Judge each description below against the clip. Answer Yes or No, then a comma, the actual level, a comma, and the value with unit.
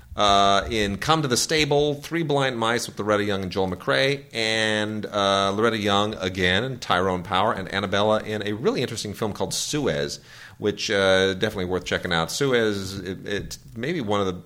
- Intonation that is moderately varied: Yes, average, 3.0 semitones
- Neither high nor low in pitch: No, low, 105 Hz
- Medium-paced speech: Yes, average, 185 wpm